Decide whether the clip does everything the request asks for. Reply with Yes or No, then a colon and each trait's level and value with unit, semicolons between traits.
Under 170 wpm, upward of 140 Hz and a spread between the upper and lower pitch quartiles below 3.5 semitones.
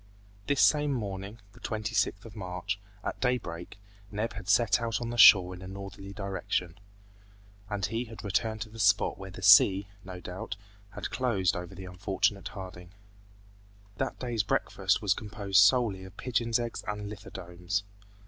No: average, 160 wpm; low, 100 Hz; average, 3.0 semitones